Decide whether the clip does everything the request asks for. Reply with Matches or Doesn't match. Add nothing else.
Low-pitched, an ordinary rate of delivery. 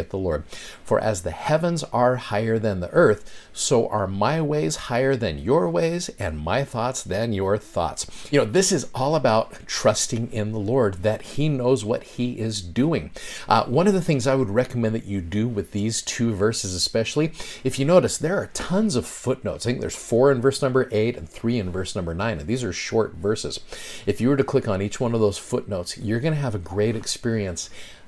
Doesn't match